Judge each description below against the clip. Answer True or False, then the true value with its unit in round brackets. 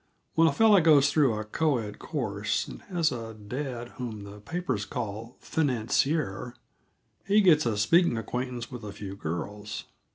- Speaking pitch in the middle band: False (120 Hz)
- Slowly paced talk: False (160 wpm)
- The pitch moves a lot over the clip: True (6.5 semitones)